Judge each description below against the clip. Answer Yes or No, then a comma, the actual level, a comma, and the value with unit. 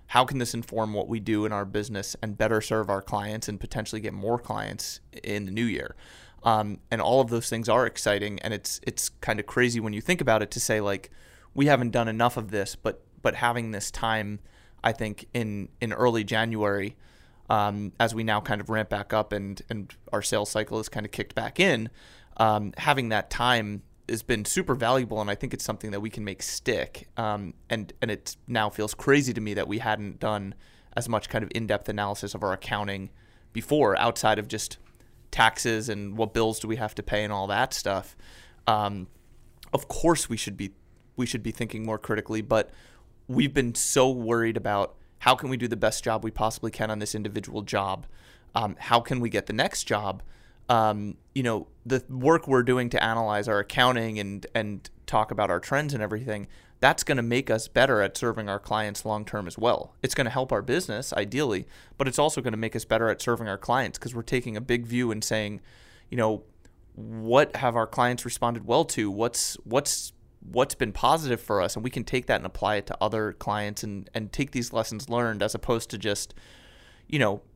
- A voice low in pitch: Yes, low, 110 Hz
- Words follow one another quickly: Yes, fast, 215 wpm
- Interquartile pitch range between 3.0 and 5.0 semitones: No, narrow, 2.4 semitones